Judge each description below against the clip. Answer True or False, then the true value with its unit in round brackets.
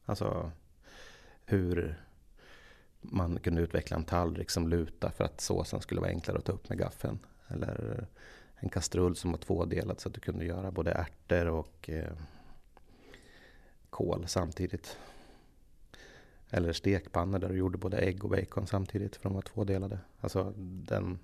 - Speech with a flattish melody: True (2.3 semitones)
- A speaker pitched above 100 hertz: False (90 Hz)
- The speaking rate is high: False (145 wpm)